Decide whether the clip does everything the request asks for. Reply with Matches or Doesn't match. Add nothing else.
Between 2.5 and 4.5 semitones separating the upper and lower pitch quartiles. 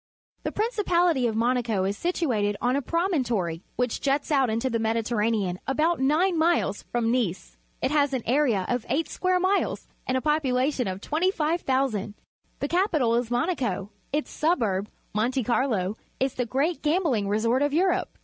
Doesn't match